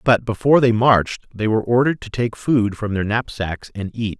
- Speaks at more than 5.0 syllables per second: Yes, 5.5 syllables/s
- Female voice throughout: No, male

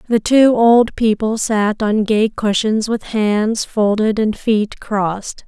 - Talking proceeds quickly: No, average, 155 wpm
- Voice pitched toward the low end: No, high, 215 Hz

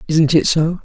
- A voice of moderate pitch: Yes, medium, 150 Hz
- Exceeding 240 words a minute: No, fast, 215 wpm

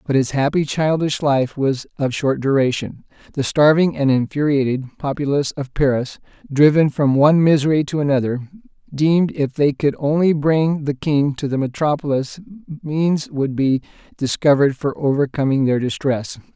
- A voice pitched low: No, medium, 145 Hz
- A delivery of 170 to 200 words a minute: No, average, 150 wpm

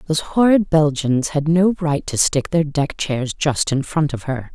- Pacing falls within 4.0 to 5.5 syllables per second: Yes, 4.4 syllables/s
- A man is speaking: No, female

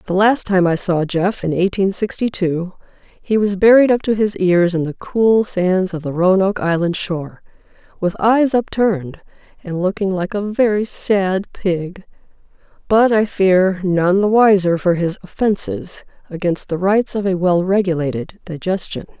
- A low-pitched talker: No, high, 190 Hz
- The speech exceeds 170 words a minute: No, average, 165 wpm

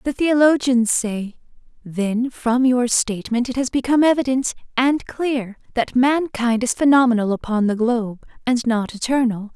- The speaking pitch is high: Yes, high, 245 Hz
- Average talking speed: Yes, average, 145 wpm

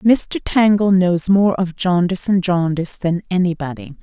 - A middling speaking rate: Yes, average, 150 wpm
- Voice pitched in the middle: Yes, medium, 180 Hz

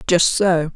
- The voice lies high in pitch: No, medium, 170 Hz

